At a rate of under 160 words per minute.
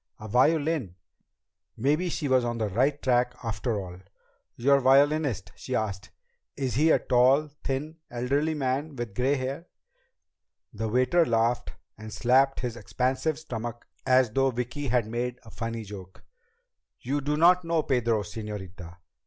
Yes: average, 145 wpm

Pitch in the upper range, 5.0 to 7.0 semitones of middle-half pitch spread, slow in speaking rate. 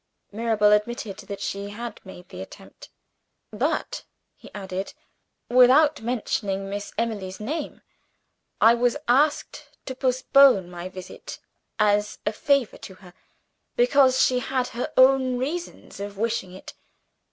No: high, 225 Hz; average, 4.4 semitones; slow, 130 wpm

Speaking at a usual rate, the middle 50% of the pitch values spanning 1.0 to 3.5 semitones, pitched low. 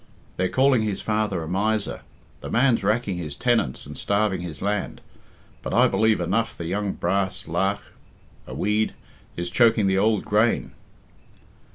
Yes: average, 155 wpm; average, 2.8 semitones; low, 100 Hz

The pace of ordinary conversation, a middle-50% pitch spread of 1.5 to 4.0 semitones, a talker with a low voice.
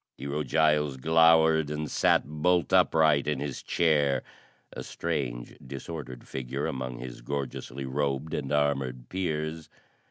No: slow, 125 wpm; average, 2.9 semitones; very low, 75 Hz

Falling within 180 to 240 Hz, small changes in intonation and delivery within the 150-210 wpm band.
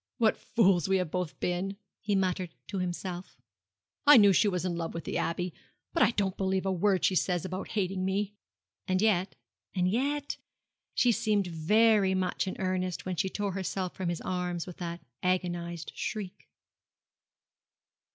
Yes: medium, 185 Hz; narrow, 2.1 semitones; average, 170 wpm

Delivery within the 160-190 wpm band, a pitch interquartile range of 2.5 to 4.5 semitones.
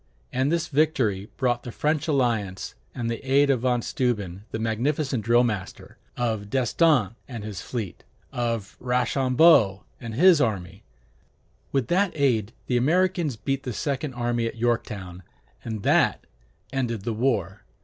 No: average, 145 wpm; average, 3.9 semitones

